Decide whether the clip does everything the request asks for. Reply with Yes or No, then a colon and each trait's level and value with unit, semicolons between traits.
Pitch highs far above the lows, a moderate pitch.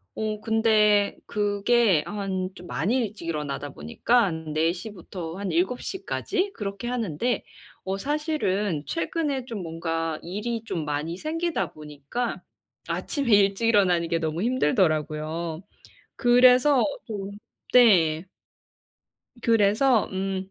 No: wide, 6.3 semitones; high, 200 Hz